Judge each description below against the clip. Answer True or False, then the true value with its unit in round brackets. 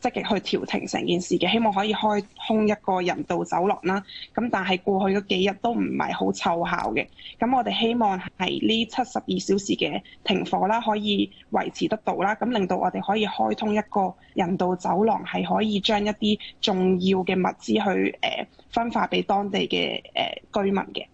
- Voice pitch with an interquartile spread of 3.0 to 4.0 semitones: False (2.5 semitones)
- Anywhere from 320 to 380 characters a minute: False (285 characters per minute)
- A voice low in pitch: False (200 Hz)